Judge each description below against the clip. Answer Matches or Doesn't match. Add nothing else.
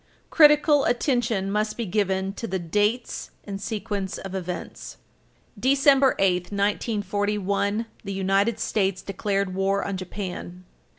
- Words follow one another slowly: Matches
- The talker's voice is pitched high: Matches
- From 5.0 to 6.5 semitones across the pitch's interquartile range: Doesn't match